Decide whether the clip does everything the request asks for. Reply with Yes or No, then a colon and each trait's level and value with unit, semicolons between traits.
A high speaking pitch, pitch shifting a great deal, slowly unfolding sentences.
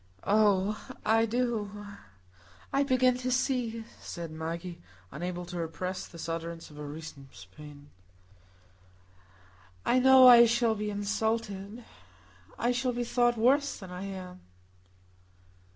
Yes: high, 205 Hz; wide, 6.1 semitones; slow, 120 wpm